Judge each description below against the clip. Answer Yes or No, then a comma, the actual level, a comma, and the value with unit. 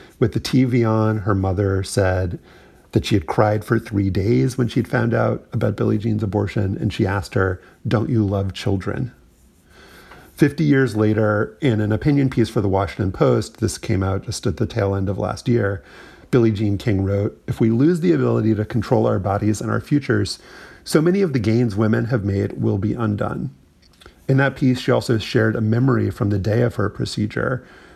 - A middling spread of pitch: Yes, average, 3.3 semitones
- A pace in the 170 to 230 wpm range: Yes, average, 200 wpm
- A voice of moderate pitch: No, low, 110 Hz